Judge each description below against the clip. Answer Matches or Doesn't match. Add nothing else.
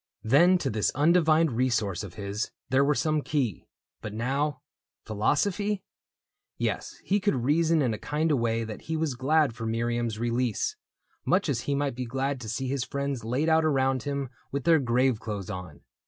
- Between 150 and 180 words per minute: Doesn't match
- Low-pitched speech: Matches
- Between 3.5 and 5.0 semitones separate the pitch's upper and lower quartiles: Matches